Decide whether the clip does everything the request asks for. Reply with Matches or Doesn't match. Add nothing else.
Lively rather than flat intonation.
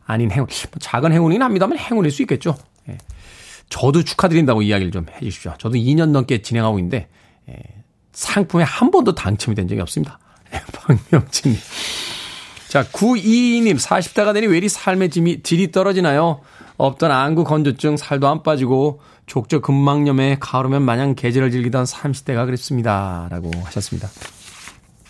Matches